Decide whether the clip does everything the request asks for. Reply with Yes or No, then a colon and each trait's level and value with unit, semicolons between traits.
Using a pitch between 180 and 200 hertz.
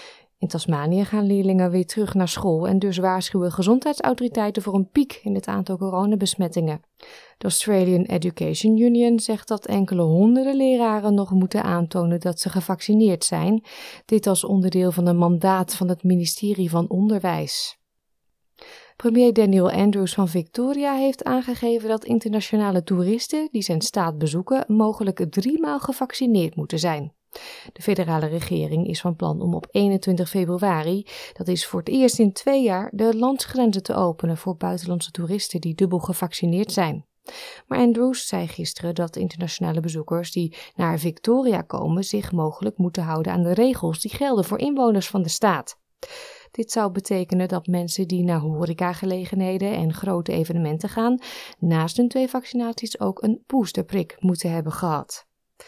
Yes: high, 190 Hz